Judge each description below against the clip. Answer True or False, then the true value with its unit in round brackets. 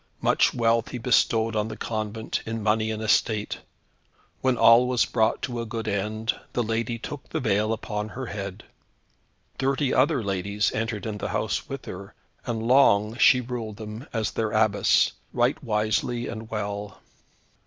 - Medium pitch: False (110 Hz)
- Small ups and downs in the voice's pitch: True (1.8 semitones)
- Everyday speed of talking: True (165 wpm)